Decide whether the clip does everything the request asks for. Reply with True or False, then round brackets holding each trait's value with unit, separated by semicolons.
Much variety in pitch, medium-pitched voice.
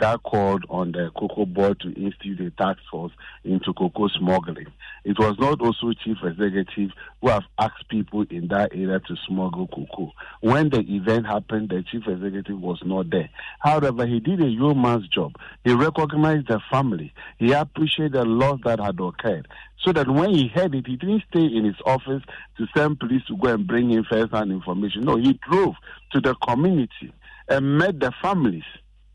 False (5.7 semitones; 110 Hz)